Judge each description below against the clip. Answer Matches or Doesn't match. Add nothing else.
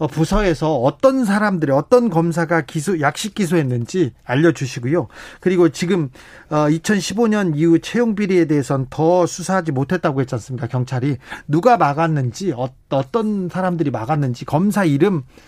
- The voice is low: Doesn't match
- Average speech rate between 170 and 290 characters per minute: Doesn't match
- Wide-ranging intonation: Doesn't match